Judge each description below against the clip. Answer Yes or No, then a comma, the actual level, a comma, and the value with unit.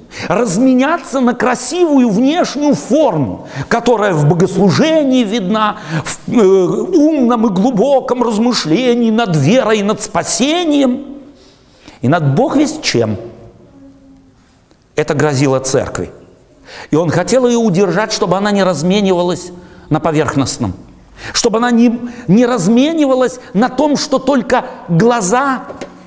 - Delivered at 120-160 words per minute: No, slow, 110 wpm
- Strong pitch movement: Yes, wide, 6.5 semitones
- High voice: Yes, high, 230 Hz